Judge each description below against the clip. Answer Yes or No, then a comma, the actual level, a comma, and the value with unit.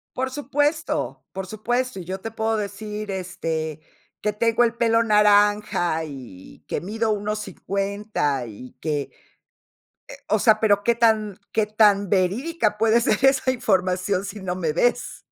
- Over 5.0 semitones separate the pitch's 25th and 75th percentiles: No, average, 3.4 semitones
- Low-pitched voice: No, high, 210 Hz